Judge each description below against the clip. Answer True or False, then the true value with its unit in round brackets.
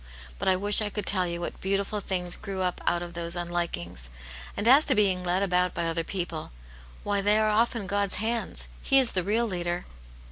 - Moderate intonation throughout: True (3.1 semitones)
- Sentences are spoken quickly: True (210 wpm)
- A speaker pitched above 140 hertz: True (190 Hz)